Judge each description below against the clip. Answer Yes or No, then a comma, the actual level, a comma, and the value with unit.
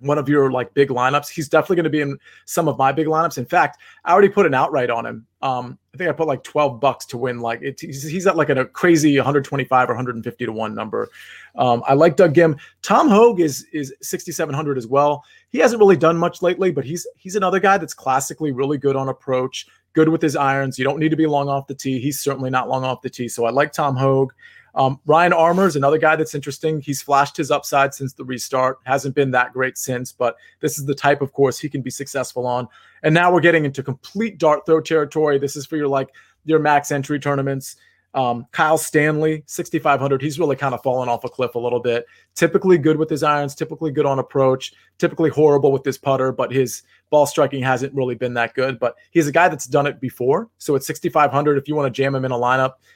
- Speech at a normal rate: No, fast, 240 wpm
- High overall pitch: No, medium, 140 Hz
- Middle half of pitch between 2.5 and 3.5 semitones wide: Yes, average, 3.2 semitones